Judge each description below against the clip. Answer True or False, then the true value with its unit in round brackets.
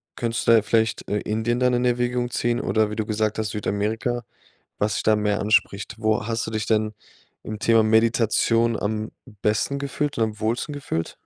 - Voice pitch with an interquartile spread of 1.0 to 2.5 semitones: True (1.8 semitones)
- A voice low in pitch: True (110 Hz)